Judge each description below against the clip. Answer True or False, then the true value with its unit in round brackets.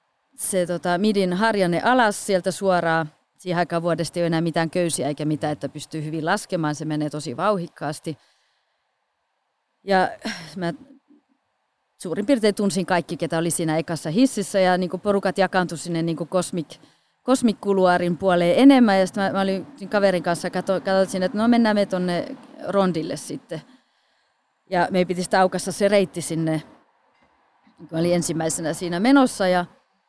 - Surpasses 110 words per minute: True (155 wpm)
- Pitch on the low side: False (180 Hz)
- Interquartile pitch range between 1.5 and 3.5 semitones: True (3.2 semitones)